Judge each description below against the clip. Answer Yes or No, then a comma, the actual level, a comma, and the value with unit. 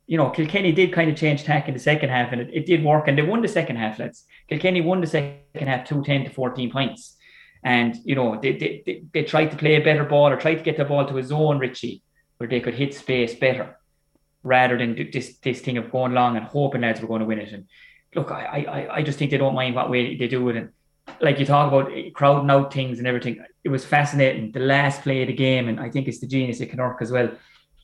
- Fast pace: Yes, fast, 265 wpm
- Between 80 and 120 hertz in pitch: No, low, 135 Hz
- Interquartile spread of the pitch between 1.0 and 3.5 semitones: Yes, average, 2.9 semitones